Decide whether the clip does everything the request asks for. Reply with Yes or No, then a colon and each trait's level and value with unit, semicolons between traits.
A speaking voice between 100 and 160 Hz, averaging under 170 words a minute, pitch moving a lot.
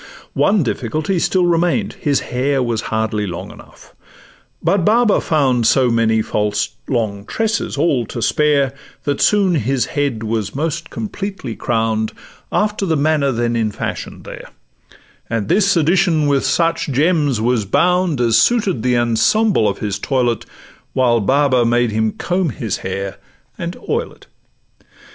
Yes: low, 135 Hz; average, 145 wpm; wide, 7.0 semitones